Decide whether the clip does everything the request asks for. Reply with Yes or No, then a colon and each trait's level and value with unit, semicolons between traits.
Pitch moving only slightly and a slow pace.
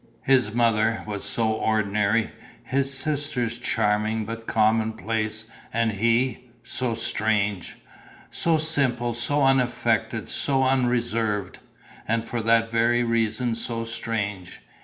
Yes: narrow, 1.9 semitones; slow, 110 wpm